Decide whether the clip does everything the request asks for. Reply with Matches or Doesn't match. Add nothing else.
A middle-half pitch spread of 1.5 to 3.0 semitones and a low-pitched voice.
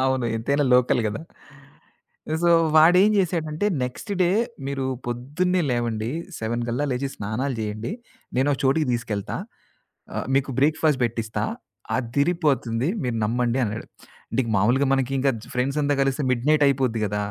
Doesn't match